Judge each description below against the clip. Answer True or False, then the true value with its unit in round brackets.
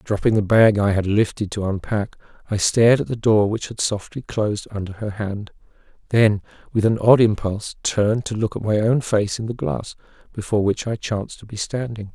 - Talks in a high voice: False (105 Hz)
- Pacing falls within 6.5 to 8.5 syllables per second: False (5.4 syllables/s)